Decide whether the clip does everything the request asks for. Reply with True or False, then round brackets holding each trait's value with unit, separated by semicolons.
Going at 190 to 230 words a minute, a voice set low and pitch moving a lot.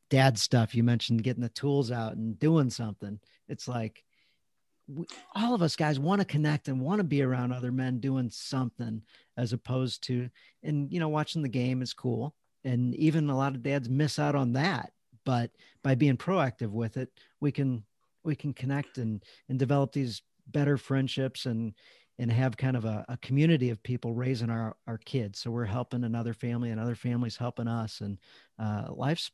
False (195 wpm; 125 Hz; 3.2 semitones)